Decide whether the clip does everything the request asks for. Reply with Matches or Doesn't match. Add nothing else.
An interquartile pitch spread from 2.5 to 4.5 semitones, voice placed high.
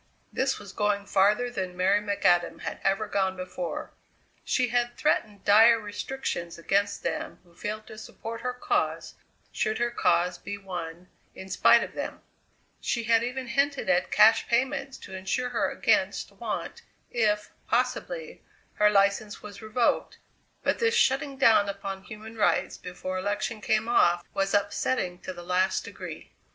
Matches